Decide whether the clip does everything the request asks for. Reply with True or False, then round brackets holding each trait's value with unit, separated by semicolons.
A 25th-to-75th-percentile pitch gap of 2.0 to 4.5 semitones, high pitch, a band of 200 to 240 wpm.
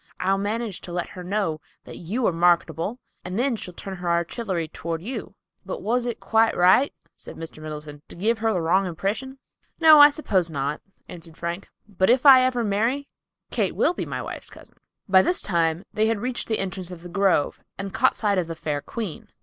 False (5.0 semitones; 195 Hz; 205 wpm)